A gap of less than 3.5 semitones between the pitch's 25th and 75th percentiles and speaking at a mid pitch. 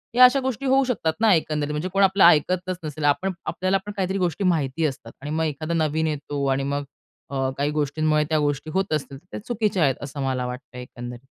No: average, 4.8 semitones; medium, 155 Hz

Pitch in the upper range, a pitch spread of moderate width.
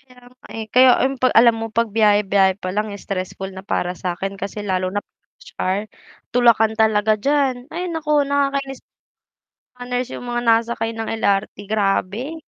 Yes: high, 225 Hz; average, 4.2 semitones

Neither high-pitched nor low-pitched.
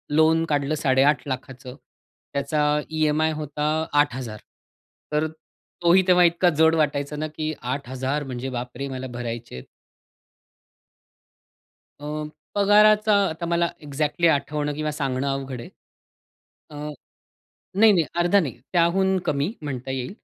Yes: medium, 150 Hz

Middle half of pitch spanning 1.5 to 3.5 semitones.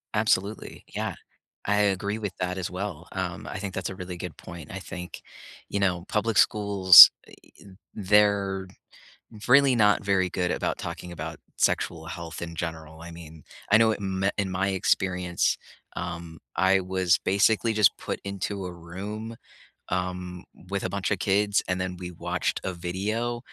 Yes: narrow, 2.5 semitones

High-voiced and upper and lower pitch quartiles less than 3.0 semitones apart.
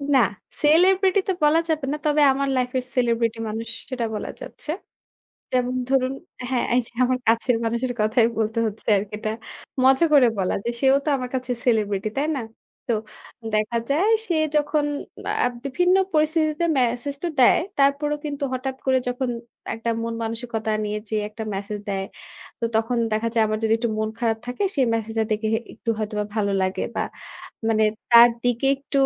No: high, 245 Hz; average, 3.9 semitones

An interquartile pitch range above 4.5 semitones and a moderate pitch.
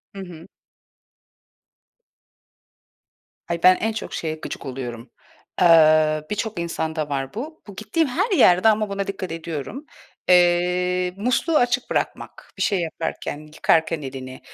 Yes: average, 5.2 semitones; medium, 180 Hz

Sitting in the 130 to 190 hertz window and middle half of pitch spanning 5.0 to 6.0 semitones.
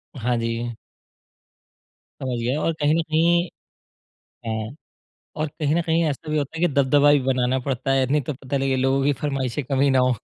No: low, 135 Hz; average, 2.8 semitones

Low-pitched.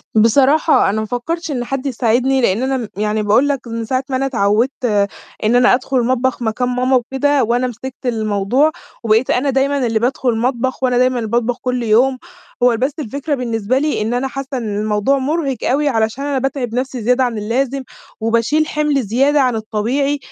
No: very high, 250 Hz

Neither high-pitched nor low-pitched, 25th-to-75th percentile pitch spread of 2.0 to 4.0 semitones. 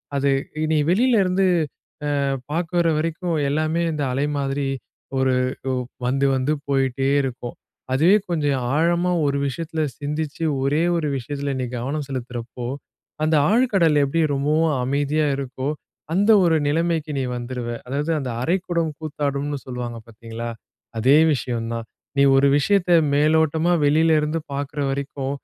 Yes: medium, 145 Hz; average, 3.3 semitones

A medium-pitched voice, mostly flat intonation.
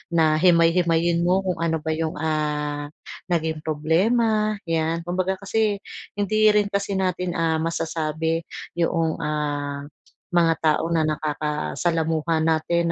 Yes: medium, 165 Hz; narrow, 2.3 semitones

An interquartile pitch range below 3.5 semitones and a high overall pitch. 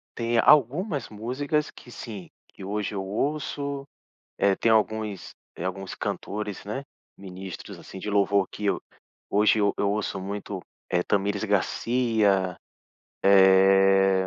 No: average, 3.0 semitones; low, 100 Hz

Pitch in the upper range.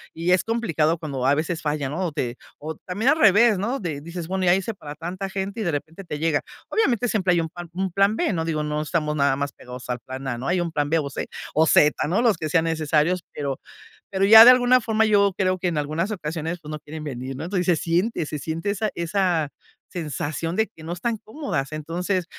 No: medium, 170 Hz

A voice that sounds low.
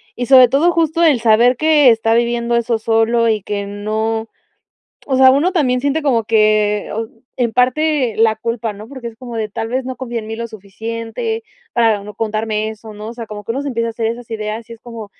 No: high, 230 Hz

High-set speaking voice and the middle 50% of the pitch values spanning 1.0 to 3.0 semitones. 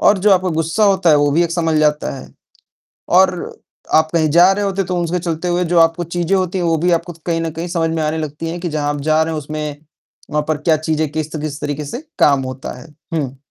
No: medium, 165 Hz; narrow, 2.4 semitones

